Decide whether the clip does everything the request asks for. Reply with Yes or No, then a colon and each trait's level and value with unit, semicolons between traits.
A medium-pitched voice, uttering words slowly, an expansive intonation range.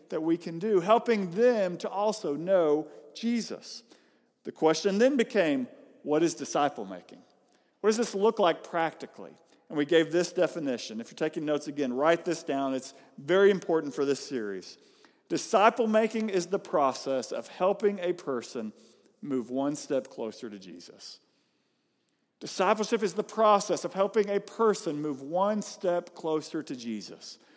No: medium, 180 Hz; average, 155 wpm; wide, 6.2 semitones